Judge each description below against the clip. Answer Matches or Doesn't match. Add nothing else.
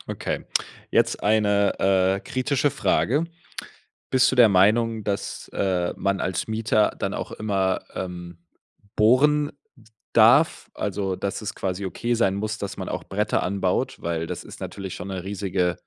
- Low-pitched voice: Matches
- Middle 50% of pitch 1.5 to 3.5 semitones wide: Matches